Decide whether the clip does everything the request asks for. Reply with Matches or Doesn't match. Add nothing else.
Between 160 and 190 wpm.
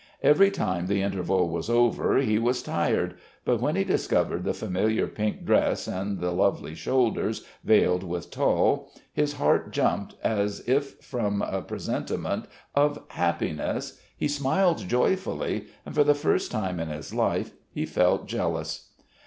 Doesn't match